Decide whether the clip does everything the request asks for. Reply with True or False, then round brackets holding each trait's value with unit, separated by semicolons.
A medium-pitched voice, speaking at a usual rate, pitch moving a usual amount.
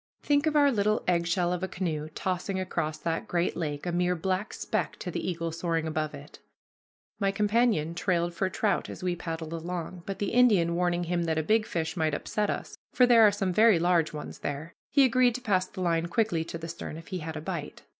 False (175 Hz; 225 wpm; 3.6 semitones)